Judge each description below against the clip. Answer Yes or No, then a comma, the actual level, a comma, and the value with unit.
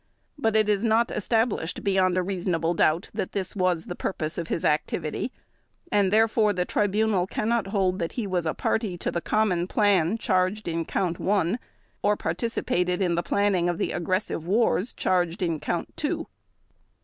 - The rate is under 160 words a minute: No, average, 175 wpm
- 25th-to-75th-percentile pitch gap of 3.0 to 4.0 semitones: Yes, average, 3.4 semitones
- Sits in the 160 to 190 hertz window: Yes, medium, 185 Hz